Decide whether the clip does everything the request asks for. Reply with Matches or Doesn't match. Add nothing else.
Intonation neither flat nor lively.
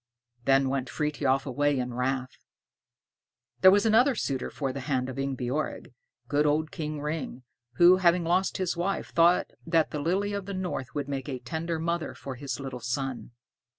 Matches